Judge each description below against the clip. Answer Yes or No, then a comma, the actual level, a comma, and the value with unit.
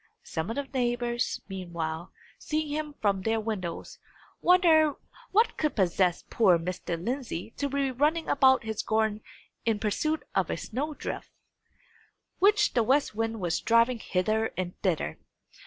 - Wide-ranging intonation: Yes, wide, 6.9 semitones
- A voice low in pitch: No, high, 225 Hz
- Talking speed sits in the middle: Yes, average, 145 wpm